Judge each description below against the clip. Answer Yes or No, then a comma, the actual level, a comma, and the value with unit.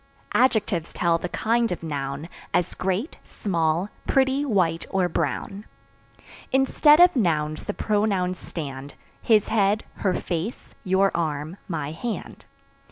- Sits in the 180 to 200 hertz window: Yes, medium, 185 Hz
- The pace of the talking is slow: Yes, slow, 125 wpm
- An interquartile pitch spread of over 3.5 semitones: Yes, average, 5.0 semitones